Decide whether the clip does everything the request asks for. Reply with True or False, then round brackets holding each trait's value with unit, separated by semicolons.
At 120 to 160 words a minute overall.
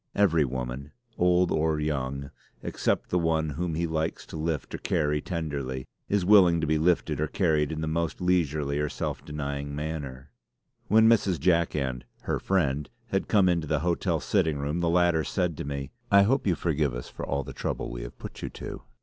False (200 wpm)